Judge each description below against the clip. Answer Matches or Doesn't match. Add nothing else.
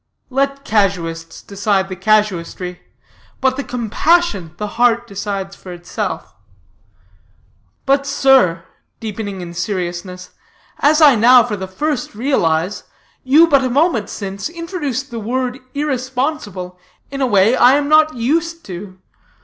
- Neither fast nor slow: Doesn't match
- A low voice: Doesn't match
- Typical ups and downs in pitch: Doesn't match